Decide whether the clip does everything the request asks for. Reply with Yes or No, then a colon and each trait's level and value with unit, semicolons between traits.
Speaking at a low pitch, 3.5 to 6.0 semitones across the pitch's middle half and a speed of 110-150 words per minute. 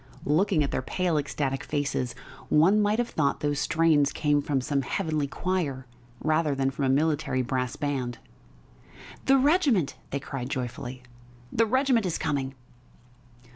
No: medium, 145 Hz; average, 4.6 semitones; average, 145 wpm